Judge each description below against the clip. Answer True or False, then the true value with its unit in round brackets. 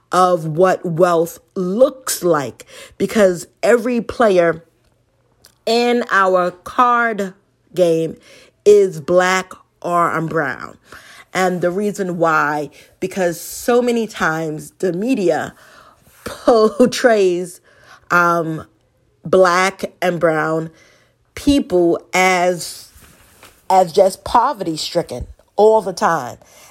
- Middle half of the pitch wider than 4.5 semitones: False (3.6 semitones)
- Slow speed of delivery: True (90 wpm)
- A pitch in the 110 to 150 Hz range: False (180 Hz)